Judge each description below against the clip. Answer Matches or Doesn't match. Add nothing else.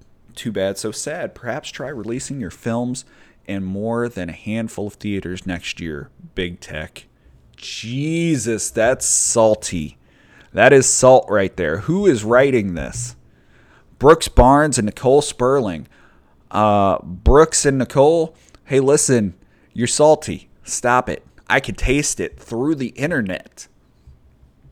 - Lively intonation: Matches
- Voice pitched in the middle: Doesn't match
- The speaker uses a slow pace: Matches